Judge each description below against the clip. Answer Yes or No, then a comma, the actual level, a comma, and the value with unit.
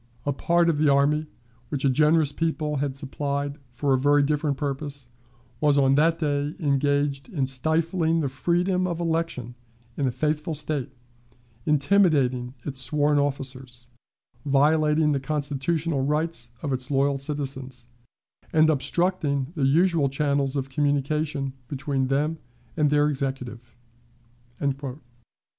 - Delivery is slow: Yes, slow, 130 wpm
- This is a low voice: No, medium, 145 Hz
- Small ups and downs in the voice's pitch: Yes, narrow, 2.3 semitones